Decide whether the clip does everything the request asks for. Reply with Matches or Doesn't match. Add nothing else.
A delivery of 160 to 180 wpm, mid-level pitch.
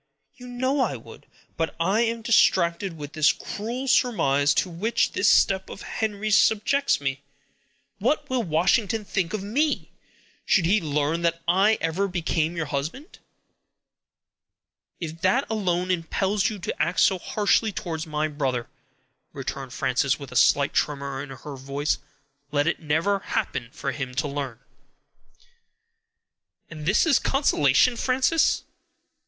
Doesn't match